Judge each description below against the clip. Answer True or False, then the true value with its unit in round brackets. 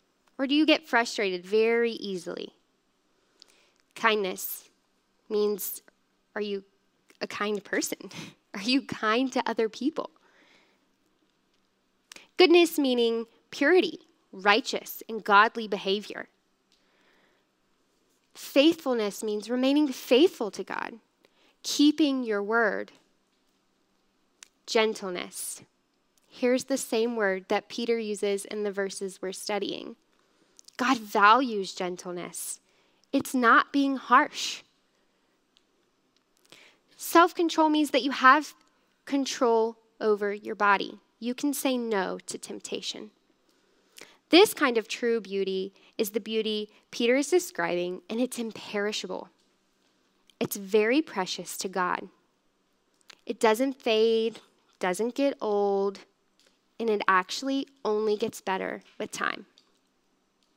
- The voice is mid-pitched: False (225 Hz)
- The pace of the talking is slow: True (105 wpm)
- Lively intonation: False (4.6 semitones)